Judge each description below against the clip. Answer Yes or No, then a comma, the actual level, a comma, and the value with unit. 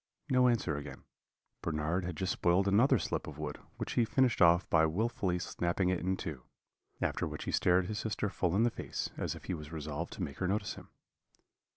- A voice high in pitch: No, very low, 90 Hz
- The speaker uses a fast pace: Yes, fast, 210 wpm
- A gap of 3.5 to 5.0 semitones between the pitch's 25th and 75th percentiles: Yes, average, 4.6 semitones